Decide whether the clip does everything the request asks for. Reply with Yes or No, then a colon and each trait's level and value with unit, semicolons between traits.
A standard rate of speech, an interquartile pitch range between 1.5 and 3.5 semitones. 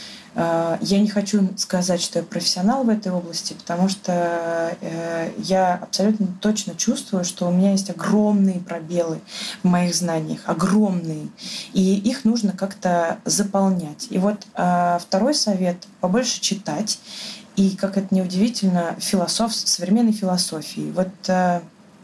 Yes: average, 125 wpm; average, 2.9 semitones